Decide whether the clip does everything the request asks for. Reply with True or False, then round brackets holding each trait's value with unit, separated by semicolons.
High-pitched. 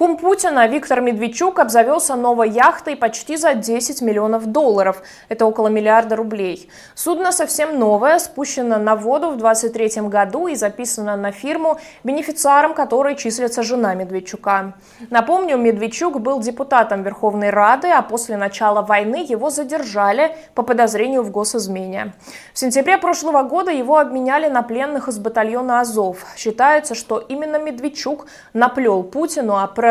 True (245 Hz)